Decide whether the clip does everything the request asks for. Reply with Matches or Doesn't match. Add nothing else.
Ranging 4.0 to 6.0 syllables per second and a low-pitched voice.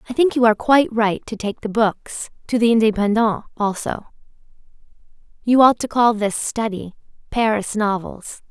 Doesn't match